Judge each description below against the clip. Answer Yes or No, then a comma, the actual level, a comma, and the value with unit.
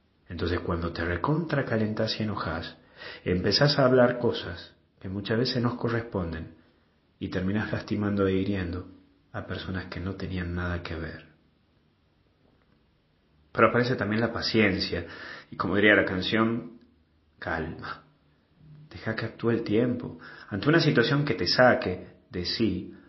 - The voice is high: No, low, 100 Hz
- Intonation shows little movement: No, average, 4.7 semitones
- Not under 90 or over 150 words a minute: Yes, average, 135 wpm